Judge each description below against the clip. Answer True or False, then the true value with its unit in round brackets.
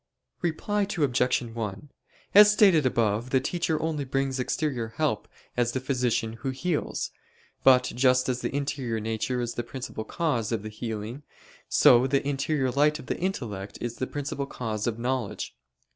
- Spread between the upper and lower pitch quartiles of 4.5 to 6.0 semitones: False (3.7 semitones)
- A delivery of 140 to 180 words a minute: True (160 wpm)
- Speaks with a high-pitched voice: False (130 Hz)